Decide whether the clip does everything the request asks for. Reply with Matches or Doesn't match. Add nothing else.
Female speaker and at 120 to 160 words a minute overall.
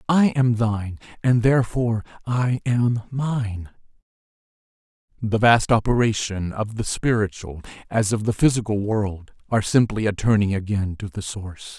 Doesn't match